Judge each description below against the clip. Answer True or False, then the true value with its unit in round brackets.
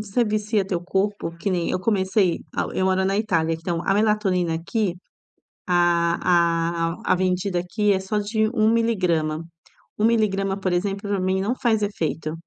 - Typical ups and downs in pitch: True (3.3 semitones)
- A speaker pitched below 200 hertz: True (190 Hz)